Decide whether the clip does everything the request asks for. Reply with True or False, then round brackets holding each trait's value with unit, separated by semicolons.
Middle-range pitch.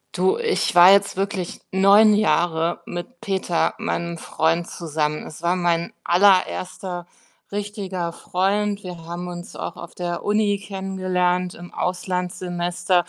True (180 Hz)